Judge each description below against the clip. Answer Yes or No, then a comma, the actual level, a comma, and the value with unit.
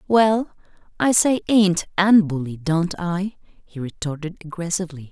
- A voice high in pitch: No, medium, 180 Hz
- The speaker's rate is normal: No, slow, 130 wpm